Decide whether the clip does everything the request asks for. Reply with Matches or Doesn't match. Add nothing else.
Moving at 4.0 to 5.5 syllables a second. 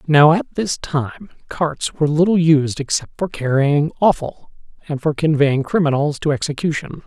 Matches